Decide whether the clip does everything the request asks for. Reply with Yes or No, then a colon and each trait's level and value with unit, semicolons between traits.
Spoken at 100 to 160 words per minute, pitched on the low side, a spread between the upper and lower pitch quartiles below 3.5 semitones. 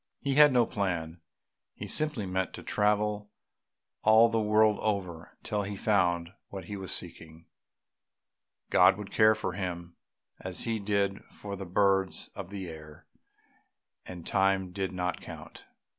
Yes: average, 145 wpm; very low, 95 Hz; average, 2.8 semitones